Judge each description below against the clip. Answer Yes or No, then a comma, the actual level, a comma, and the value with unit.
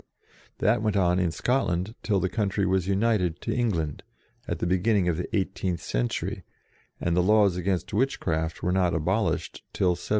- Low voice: Yes, very low, 95 Hz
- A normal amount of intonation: Yes, average, 3.1 semitones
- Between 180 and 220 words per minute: No, average, 170 wpm